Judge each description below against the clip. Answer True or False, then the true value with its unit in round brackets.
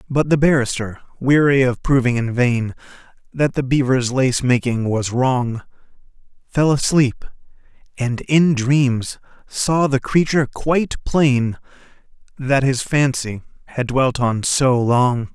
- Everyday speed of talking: False (130 wpm)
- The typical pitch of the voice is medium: False (130 Hz)